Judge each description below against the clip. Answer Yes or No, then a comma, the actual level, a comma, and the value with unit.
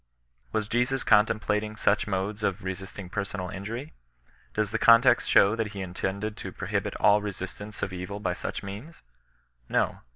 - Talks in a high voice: No, low, 105 Hz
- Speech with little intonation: Yes, narrow, 1.9 semitones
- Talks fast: No, average, 160 wpm